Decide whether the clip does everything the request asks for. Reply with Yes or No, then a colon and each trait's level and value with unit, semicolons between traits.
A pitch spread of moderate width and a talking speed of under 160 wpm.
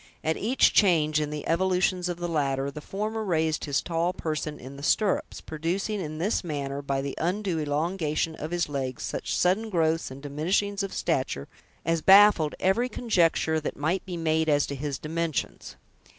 No: average, 3.8 semitones; average, 180 wpm